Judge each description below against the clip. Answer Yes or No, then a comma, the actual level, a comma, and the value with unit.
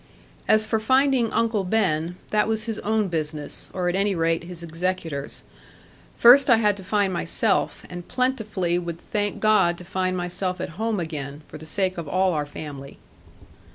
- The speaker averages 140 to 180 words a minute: Yes, average, 175 wpm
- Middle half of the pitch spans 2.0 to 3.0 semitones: No, average, 4.3 semitones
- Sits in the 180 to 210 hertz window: Yes, medium, 185 Hz